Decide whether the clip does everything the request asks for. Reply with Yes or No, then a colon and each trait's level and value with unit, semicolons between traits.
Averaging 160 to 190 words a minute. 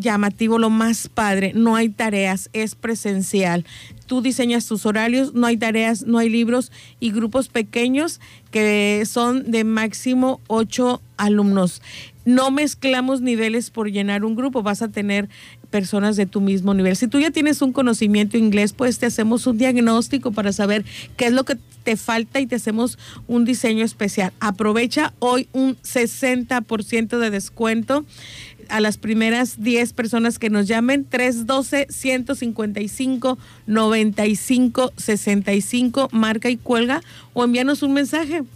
No: average, 145 wpm